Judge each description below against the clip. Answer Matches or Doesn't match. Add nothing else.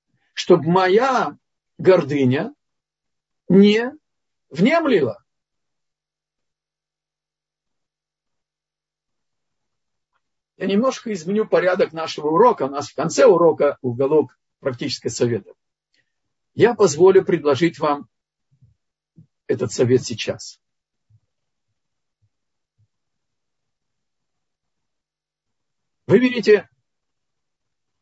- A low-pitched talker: Doesn't match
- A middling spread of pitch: Doesn't match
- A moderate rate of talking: Doesn't match